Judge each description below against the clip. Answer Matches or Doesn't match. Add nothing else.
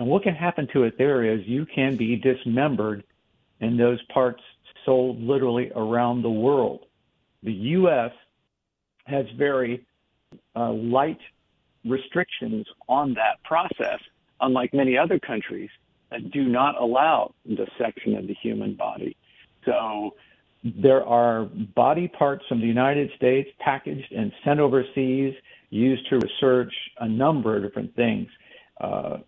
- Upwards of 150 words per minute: Doesn't match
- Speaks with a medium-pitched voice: Doesn't match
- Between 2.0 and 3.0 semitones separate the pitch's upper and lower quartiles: Matches